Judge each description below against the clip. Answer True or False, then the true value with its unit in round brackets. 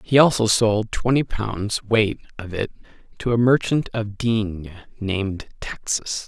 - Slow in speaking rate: False (145 wpm)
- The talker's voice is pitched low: True (110 Hz)